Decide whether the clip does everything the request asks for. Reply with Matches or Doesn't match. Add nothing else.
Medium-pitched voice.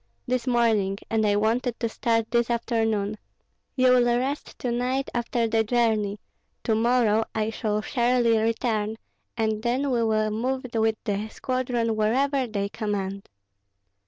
Doesn't match